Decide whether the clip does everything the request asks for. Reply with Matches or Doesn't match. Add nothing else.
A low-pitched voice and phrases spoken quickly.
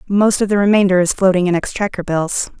Doesn't match